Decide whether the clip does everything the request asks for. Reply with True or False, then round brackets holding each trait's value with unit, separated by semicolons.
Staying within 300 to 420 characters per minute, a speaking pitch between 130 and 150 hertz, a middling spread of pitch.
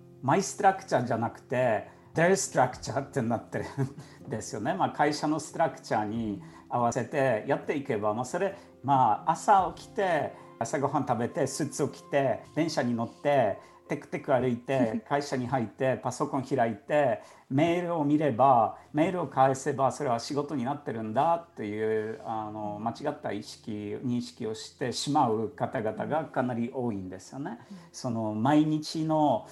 True (330 characters per minute; 135 Hz; 4.6 semitones)